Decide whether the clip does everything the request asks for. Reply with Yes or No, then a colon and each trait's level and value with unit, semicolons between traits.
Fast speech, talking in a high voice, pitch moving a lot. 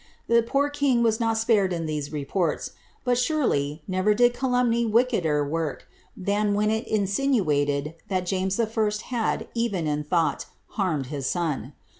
No: average, 150 wpm; high, 200 Hz; wide, 6.9 semitones